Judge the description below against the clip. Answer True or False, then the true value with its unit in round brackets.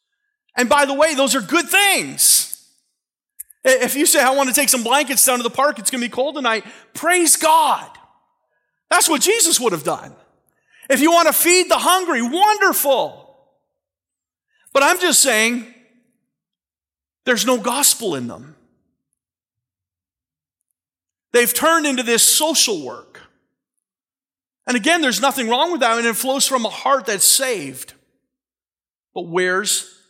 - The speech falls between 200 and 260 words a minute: False (155 wpm)